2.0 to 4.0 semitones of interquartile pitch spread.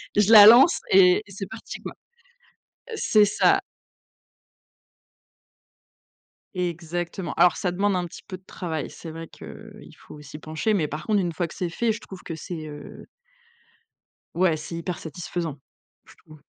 Yes: average, 3.7 semitones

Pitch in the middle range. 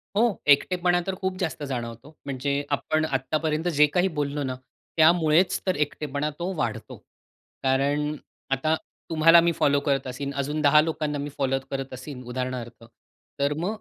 Yes: medium, 145 Hz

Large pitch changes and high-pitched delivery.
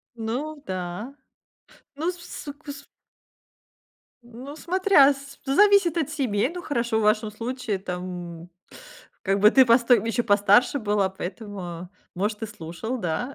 Yes: wide, 5.9 semitones; high, 230 Hz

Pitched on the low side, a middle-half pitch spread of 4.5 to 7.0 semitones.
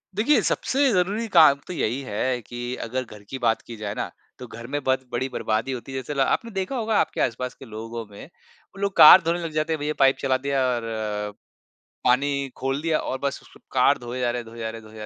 Yes: low, 130 Hz; average, 4.8 semitones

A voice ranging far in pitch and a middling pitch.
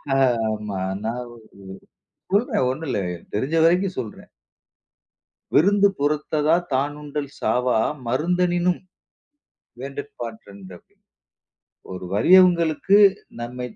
Yes: wide, 6.7 semitones; medium, 145 Hz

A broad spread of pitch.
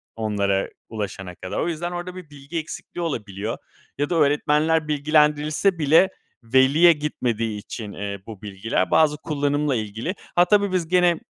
Yes: wide, 6.9 semitones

